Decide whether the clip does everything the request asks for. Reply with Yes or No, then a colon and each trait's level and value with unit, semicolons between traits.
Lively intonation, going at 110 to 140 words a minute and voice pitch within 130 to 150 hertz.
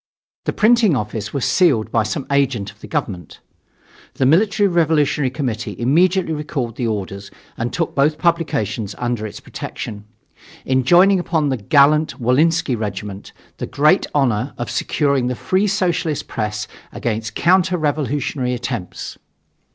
Yes: wide, 6.3 semitones; slow, 135 wpm; medium, 140 Hz